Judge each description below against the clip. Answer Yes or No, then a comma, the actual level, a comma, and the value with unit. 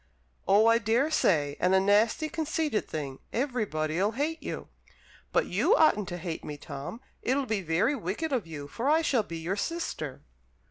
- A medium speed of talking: Yes, average, 170 wpm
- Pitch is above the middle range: Yes, high, 210 Hz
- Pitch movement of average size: No, wide, 8.8 semitones